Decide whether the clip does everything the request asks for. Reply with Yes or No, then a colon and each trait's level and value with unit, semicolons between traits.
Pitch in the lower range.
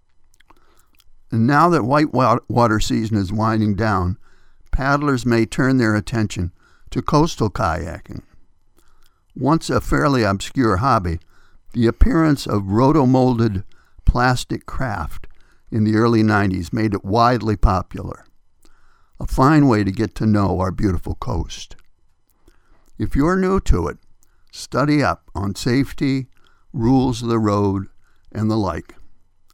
Yes: low, 110 Hz